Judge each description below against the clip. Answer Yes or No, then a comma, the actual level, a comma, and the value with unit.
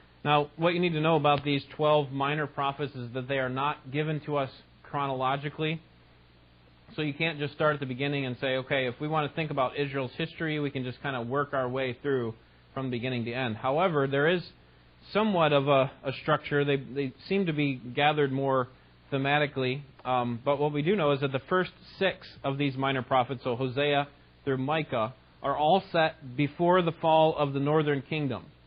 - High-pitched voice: No, medium, 140 Hz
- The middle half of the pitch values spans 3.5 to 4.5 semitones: No, narrow, 2.6 semitones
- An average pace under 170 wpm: No, fast, 205 wpm